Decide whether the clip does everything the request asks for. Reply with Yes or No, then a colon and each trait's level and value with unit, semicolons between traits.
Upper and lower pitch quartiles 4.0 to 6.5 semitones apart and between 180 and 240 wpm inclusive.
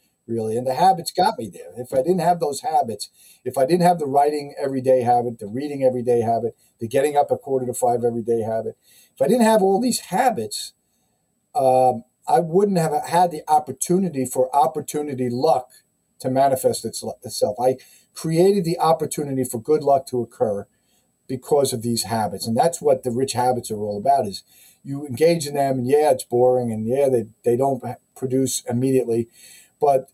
Yes: average, 5.1 semitones; average, 185 wpm